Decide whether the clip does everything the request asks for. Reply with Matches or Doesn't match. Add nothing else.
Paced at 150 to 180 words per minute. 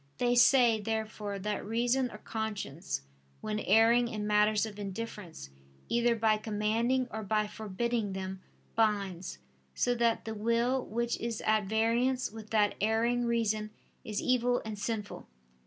Doesn't match